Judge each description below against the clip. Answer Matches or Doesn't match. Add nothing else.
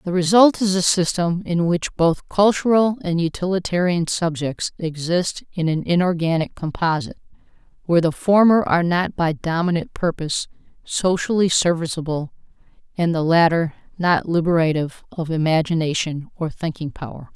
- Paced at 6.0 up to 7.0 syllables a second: Doesn't match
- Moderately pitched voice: Matches